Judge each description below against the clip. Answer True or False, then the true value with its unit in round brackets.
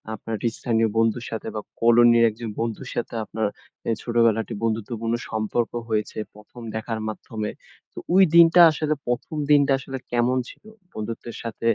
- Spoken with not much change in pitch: True (1.6 semitones)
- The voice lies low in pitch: True (115 Hz)